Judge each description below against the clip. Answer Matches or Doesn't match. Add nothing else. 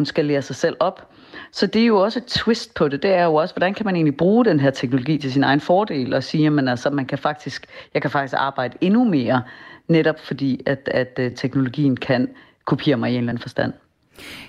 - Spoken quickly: Matches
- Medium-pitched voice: Matches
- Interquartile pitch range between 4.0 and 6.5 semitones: Matches